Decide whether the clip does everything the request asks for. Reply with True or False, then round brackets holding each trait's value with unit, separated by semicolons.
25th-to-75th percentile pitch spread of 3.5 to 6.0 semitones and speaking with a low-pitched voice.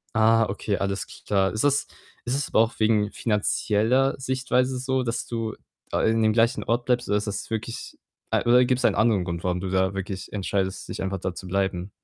True (3.9 semitones; 110 Hz)